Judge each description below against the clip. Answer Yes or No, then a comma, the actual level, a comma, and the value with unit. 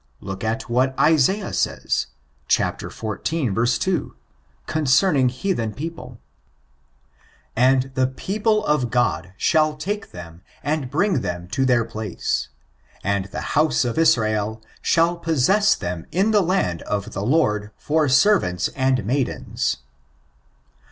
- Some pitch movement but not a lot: No, wide, 7.2 semitones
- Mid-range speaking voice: No, low, 130 Hz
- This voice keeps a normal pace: No, slow, 125 wpm